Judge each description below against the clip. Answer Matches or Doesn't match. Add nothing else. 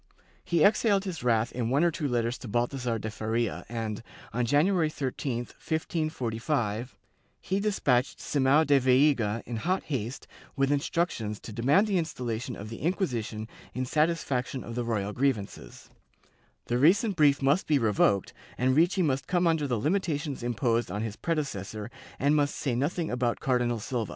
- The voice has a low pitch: Matches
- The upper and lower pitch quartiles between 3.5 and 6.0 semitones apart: Matches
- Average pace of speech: Matches